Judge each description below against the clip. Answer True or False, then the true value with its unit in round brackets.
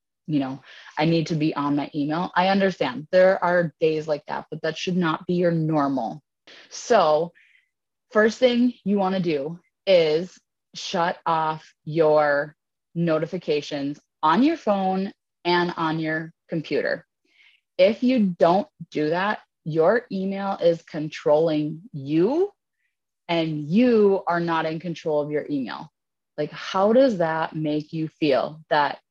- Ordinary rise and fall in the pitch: True (3.8 semitones)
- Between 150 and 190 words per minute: False (140 wpm)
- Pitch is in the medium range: True (165 Hz)